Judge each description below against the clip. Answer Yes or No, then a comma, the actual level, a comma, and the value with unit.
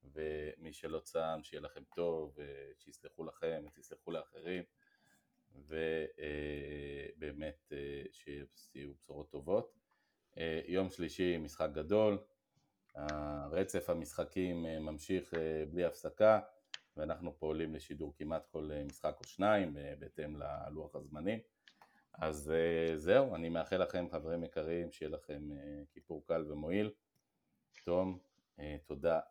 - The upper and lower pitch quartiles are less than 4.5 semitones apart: Yes, average, 3.1 semitones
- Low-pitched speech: Yes, very low, 80 Hz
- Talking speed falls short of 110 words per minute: Yes, slow, 100 wpm